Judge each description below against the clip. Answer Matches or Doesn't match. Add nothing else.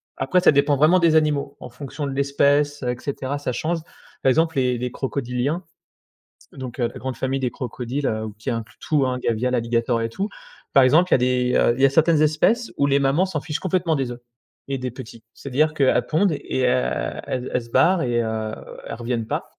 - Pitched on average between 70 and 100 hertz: Doesn't match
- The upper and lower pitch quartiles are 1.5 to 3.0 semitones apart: Doesn't match